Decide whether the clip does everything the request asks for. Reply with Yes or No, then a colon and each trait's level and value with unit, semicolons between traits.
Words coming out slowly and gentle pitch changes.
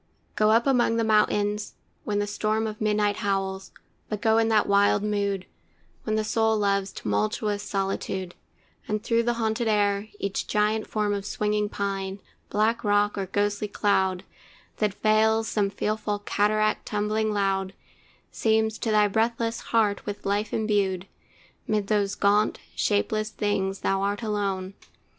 No: average, 150 wpm; narrow, 1.3 semitones